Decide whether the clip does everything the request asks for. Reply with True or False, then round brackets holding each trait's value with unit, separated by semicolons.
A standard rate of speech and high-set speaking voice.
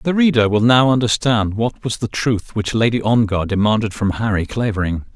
False (185 wpm; 110 Hz)